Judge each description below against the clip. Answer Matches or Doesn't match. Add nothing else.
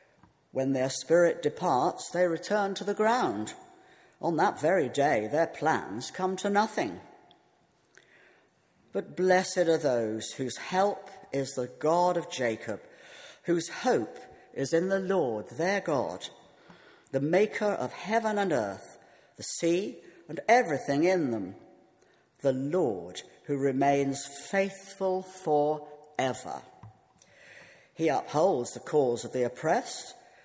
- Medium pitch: Matches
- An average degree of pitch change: Doesn't match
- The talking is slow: Matches